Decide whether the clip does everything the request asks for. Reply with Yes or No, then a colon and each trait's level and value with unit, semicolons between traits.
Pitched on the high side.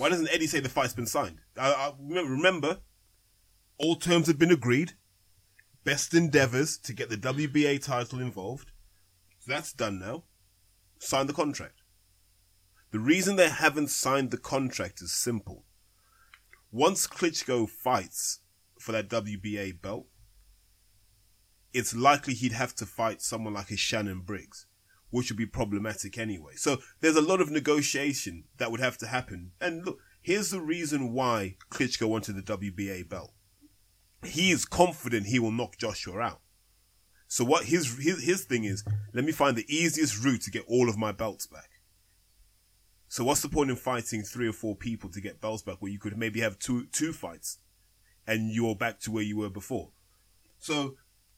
No: low, 110 Hz